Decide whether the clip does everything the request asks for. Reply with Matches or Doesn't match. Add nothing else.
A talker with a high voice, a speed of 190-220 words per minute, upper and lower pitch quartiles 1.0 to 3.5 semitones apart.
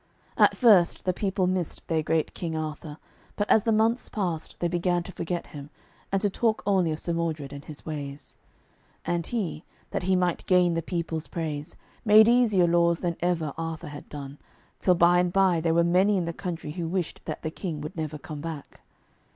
Doesn't match